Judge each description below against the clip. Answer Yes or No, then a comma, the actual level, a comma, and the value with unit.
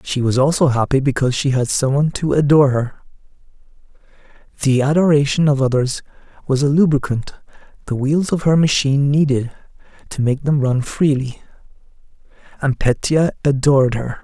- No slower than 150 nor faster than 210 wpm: No, average, 140 wpm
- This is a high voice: No, medium, 140 Hz